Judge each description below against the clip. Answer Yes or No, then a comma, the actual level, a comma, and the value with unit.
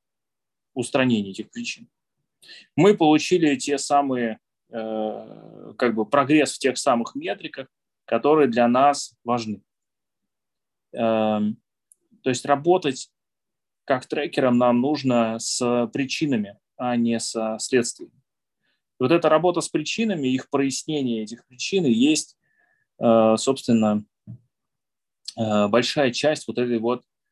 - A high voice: No, low, 130 Hz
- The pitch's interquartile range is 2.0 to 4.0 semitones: No, average, 4.4 semitones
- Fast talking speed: No, average, 115 wpm